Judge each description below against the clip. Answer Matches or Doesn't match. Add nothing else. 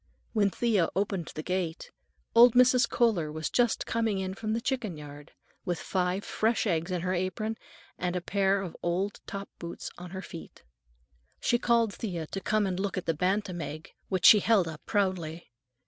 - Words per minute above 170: Matches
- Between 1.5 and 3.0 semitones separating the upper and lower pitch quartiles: Doesn't match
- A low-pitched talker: Doesn't match